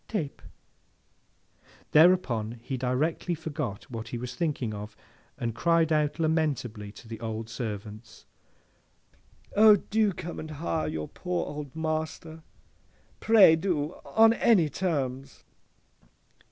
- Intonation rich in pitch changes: Yes, wide, 6.2 semitones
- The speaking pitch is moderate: Yes, medium, 150 Hz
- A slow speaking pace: Yes, slow, 115 wpm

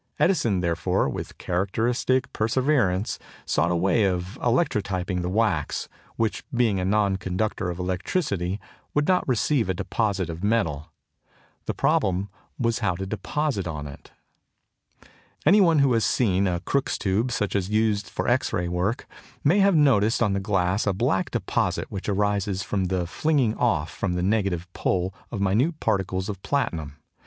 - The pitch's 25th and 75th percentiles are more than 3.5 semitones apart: Yes, average, 4.2 semitones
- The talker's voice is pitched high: No, low, 100 Hz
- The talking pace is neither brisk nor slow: Yes, average, 165 wpm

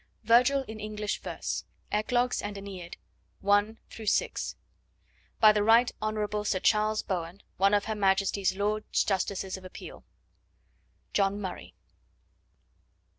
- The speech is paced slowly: Yes, slow, 120 wpm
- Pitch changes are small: Yes, narrow, 1.7 semitones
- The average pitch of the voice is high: Yes, high, 210 Hz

